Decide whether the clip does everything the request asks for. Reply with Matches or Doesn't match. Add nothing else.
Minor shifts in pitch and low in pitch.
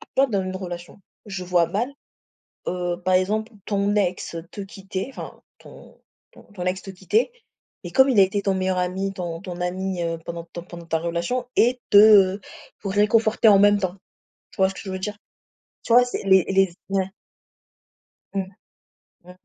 Doesn't match